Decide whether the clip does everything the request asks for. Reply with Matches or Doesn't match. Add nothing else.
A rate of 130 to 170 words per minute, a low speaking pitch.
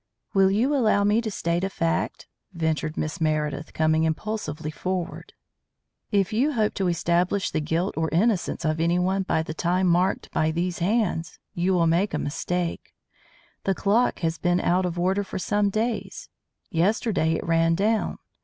Doesn't match